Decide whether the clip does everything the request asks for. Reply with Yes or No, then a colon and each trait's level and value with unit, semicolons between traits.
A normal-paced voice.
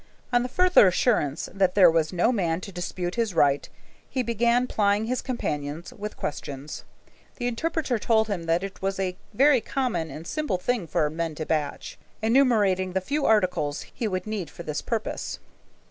Yes: average, 175 wpm